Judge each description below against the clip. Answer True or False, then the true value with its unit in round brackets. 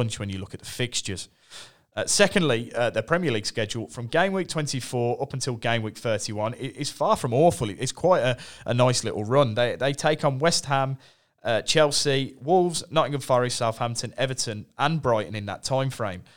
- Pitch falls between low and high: False (130 Hz)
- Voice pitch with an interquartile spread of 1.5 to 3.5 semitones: False (4.3 semitones)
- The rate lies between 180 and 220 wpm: True (190 wpm)